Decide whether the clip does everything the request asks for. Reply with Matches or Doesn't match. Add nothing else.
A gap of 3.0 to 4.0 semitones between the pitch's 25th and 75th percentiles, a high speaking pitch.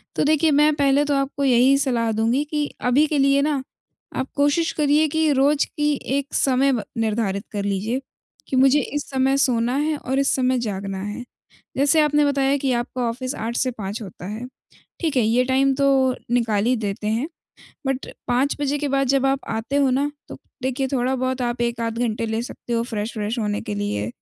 Matches